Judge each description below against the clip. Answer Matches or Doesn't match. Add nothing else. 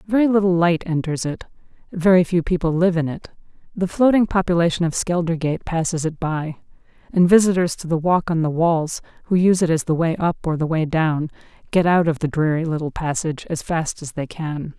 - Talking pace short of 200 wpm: Doesn't match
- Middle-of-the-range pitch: Matches